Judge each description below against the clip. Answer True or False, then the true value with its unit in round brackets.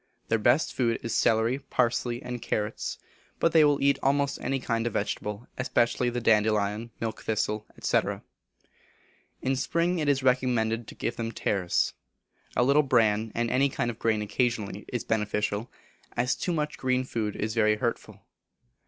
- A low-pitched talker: True (120 Hz)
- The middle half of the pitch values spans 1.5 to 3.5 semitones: True (3.2 semitones)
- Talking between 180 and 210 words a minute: False (160 wpm)